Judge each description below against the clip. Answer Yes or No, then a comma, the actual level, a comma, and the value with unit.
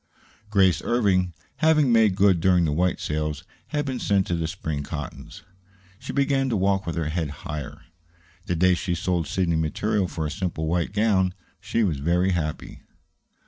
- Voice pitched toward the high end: No, very low, 90 Hz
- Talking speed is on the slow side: No, average, 175 wpm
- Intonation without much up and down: No, average, 4.1 semitones